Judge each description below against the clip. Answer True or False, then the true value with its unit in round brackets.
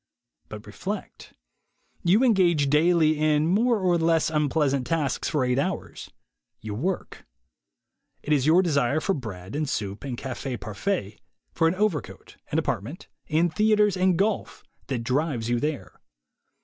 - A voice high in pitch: False (155 Hz)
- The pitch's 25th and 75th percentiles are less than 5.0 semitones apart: False (5.3 semitones)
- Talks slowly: False (145 wpm)